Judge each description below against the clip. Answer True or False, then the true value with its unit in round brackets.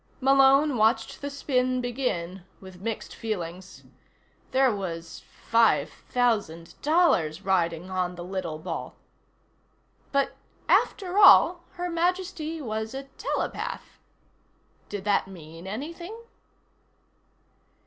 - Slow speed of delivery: True (100 wpm)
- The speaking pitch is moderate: False (225 Hz)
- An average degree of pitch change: False (7.4 semitones)